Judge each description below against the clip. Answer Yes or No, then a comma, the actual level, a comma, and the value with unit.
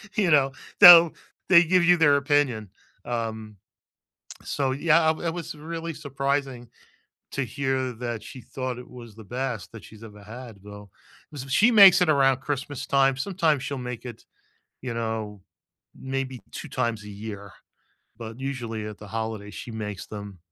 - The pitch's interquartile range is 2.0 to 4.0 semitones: No, average, 4.6 semitones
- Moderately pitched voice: No, low, 130 Hz